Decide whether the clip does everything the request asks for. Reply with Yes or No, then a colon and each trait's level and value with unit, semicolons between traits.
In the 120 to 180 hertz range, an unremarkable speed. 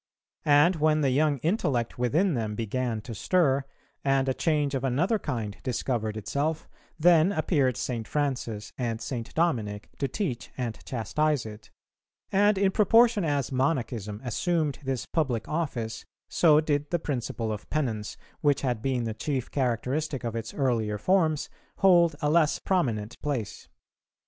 Yes: low, 135 Hz; average, 150 wpm